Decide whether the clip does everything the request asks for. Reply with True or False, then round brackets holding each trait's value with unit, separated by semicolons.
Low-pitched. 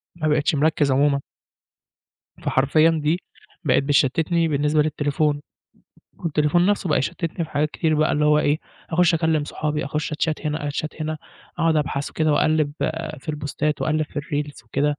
False (150 Hz)